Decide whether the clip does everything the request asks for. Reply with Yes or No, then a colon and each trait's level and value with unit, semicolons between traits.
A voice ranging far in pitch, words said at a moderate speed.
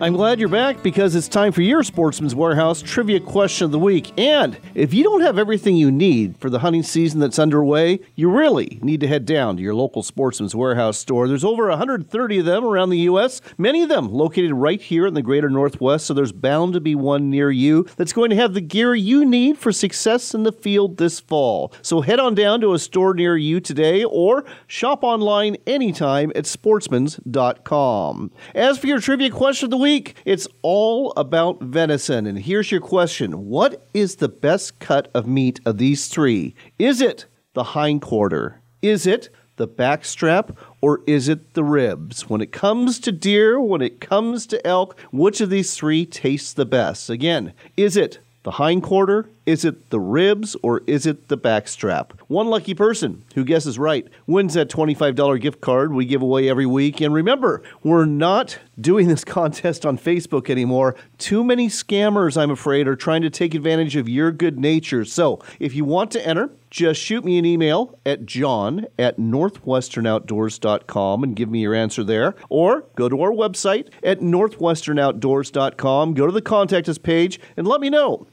Yes: wide, 6.5 semitones; average, 190 wpm